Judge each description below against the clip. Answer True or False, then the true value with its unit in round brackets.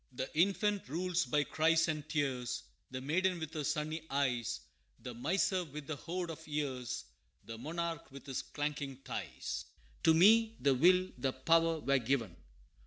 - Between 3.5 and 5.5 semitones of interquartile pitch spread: True (3.9 semitones)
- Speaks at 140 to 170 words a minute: True (160 wpm)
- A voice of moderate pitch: True (150 Hz)